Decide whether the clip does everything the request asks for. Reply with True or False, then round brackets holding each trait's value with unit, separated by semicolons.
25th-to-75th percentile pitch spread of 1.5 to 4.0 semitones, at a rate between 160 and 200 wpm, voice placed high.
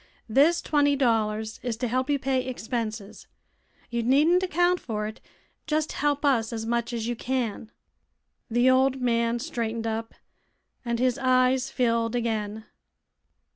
False (2.8 semitones; 140 wpm; 240 Hz)